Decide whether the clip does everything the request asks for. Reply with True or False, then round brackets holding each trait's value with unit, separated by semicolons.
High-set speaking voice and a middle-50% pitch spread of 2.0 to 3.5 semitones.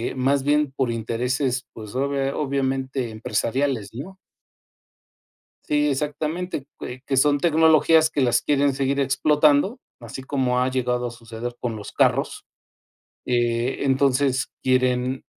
False (135 Hz; 2.5 semitones)